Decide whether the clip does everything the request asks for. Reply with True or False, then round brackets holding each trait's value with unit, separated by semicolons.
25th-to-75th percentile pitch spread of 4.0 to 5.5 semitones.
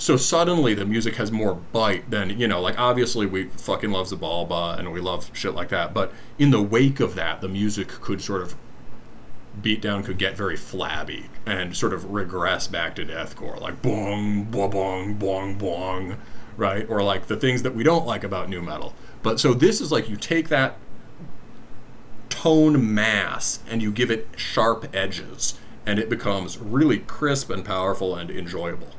False (3.5 semitones)